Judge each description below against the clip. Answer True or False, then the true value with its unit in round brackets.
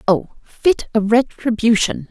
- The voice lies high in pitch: True (225 Hz)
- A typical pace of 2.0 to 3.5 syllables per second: True (3.4 syllables/s)